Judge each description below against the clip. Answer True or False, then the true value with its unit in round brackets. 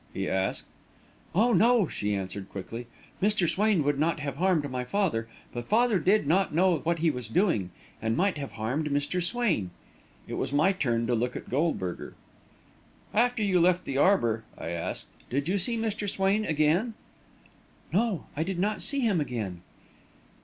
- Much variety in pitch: True (8.1 semitones)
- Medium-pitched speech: True (165 Hz)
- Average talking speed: True (170 wpm)